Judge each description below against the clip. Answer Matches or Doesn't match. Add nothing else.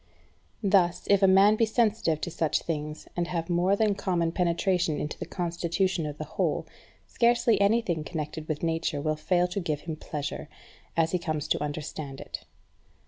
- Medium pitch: Matches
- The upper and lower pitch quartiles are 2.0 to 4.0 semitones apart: Matches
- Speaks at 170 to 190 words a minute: Matches